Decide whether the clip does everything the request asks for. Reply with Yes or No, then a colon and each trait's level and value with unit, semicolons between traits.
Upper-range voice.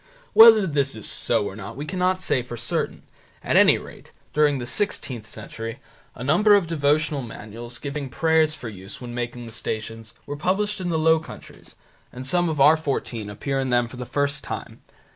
No: medium, 140 Hz